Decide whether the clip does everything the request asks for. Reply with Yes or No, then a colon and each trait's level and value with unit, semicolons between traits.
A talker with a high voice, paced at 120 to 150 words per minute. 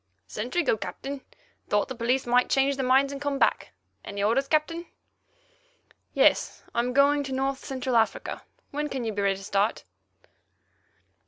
No: very high, 265 Hz; average, 165 wpm